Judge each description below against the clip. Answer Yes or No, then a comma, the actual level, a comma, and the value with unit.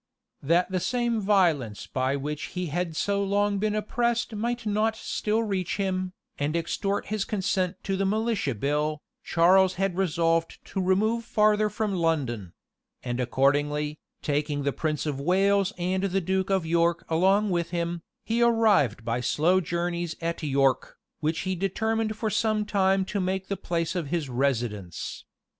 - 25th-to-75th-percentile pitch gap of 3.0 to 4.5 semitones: No, average, 5.0 semitones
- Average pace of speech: Yes, average, 160 wpm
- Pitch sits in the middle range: Yes, medium, 180 Hz